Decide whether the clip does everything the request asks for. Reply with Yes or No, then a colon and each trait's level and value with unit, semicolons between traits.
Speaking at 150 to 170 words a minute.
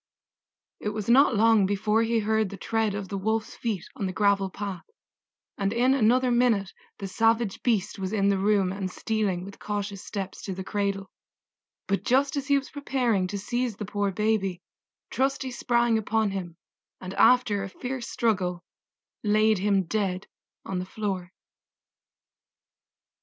Yes: average, 160 wpm